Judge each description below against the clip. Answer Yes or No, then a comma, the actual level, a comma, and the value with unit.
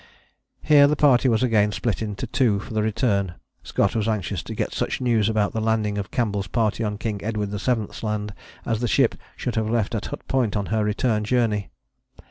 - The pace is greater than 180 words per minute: Yes, fast, 205 wpm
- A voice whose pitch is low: Yes, low, 110 Hz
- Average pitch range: No, narrow, 2.2 semitones